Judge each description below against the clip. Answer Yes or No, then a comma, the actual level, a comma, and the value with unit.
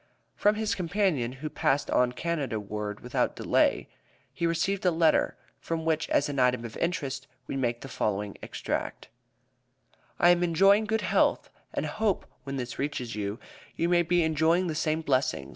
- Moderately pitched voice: Yes, medium, 155 Hz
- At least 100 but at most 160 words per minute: No, average, 170 wpm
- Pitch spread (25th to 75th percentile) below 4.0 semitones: No, wide, 5.6 semitones